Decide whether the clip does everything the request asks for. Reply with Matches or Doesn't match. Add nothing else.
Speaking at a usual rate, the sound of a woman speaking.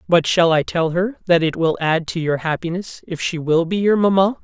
Doesn't match